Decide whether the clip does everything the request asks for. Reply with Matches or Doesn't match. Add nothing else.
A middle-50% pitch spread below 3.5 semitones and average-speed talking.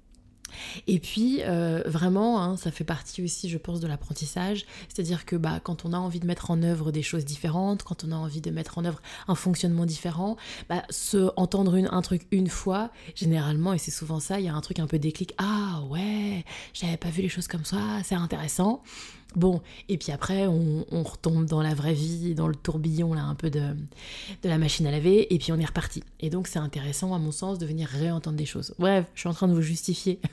Doesn't match